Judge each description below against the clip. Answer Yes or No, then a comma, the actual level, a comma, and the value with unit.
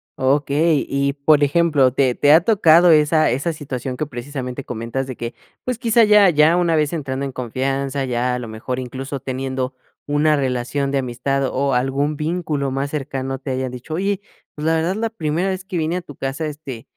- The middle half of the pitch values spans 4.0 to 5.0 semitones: No, average, 3.3 semitones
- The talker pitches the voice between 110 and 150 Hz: Yes, medium, 140 Hz